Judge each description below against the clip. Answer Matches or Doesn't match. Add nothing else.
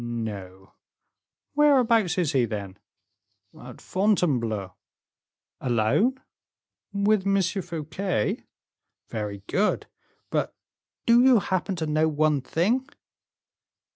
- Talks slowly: Matches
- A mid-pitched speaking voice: Matches